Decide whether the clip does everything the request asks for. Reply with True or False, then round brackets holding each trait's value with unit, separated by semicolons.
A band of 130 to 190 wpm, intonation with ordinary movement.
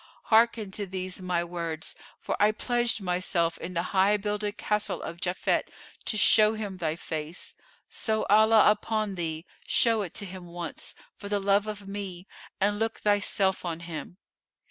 True (165 wpm; 3.2 semitones)